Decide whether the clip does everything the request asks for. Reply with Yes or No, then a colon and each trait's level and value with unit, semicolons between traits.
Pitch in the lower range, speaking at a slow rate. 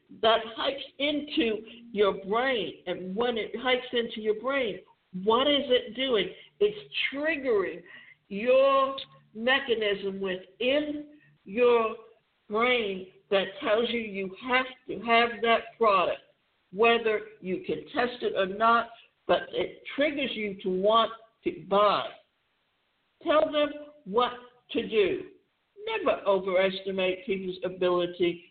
No: high, 230 Hz; slow, 120 wpm